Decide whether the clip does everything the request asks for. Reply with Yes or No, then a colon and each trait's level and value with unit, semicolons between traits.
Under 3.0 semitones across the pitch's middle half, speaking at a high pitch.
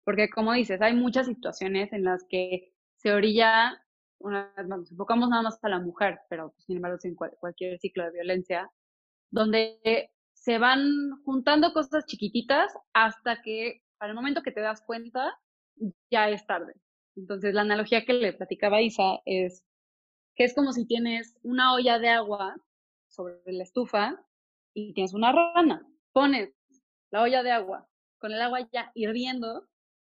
No: average, 4.1 semitones; high, 225 Hz